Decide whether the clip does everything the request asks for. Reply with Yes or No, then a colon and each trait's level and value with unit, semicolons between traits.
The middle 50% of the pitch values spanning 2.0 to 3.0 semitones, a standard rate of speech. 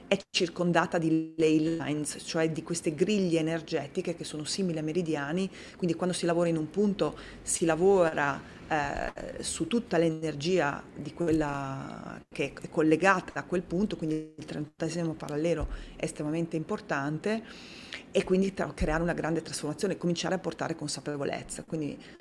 Yes: narrow, 2.6 semitones; average, 150 wpm